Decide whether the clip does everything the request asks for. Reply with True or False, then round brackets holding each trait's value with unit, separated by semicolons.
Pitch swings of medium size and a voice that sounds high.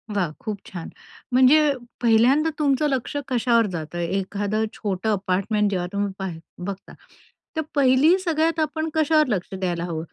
False (7.2 semitones; 220 Hz)